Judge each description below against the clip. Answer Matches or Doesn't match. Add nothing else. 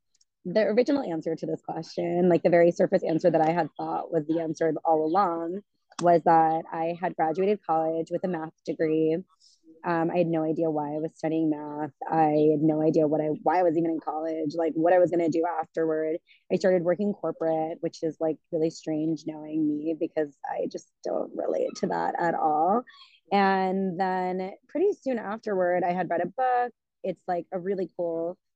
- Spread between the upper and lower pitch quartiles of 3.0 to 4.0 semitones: Doesn't match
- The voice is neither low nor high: Matches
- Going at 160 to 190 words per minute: Doesn't match